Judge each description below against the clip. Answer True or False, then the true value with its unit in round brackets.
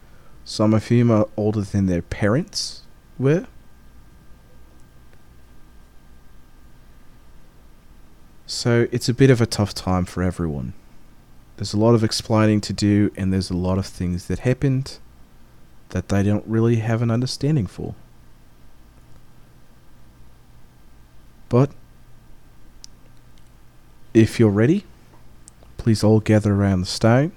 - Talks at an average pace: False (115 wpm)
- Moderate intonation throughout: False (7.9 semitones)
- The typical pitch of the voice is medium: False (105 Hz)